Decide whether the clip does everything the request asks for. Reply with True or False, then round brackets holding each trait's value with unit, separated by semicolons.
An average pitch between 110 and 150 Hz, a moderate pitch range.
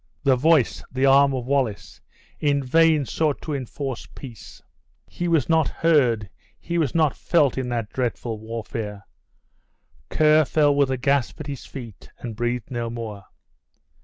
True (135 Hz; 4.1 semitones)